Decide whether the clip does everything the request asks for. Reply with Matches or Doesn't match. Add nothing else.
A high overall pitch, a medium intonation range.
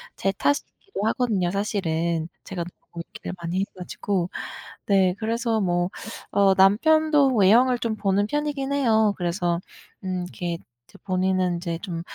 Matches